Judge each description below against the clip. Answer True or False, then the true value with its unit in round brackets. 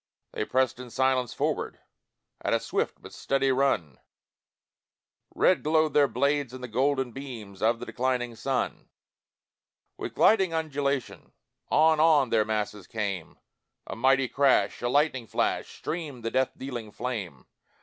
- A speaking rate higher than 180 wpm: False (140 wpm)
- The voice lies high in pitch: False (130 Hz)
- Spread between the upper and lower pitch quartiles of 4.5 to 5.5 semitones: False (3.6 semitones)